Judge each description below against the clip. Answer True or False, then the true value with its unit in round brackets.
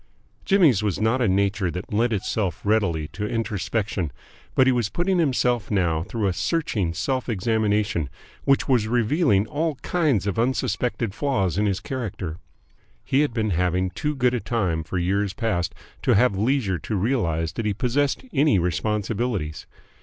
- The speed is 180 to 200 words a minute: False (160 wpm)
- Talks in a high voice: False (105 Hz)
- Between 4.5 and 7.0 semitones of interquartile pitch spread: True (4.9 semitones)